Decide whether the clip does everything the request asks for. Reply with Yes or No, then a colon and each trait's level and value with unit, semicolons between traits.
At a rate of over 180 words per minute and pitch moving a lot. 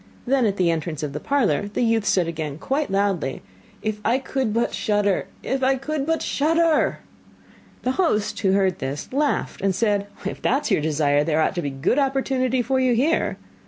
Yes: average, 200 wpm; wide, 7.5 semitones